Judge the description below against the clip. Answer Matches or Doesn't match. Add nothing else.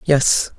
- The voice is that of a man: Doesn't match